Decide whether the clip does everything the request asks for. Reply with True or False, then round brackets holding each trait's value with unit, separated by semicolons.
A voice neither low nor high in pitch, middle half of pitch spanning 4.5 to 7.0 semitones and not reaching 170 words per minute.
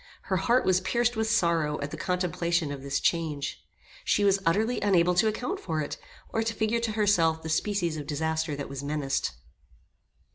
False (170 Hz; 5.3 semitones; 185 wpm)